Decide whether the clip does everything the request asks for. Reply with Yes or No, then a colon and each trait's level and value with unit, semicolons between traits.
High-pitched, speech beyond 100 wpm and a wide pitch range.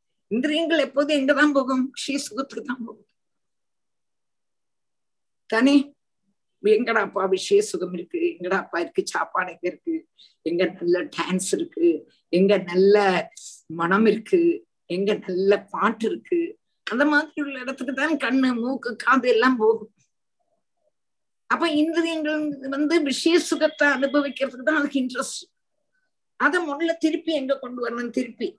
Yes: very high, 275 Hz; average, 115 wpm; wide, 6.9 semitones